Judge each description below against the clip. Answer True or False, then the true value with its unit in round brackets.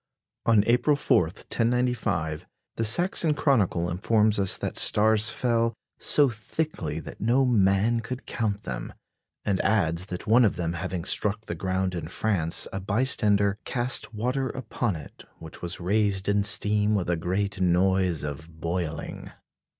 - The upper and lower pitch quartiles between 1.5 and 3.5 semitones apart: False (4.5 semitones)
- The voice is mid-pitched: False (100 Hz)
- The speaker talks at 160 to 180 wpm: False (150 wpm)